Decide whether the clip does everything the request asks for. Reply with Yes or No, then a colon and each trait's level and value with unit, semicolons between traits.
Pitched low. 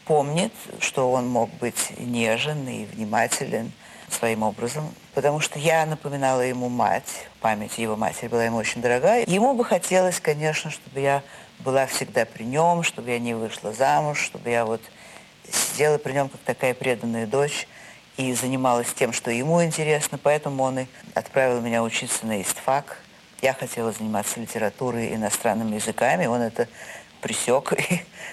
Yes: low, 130 Hz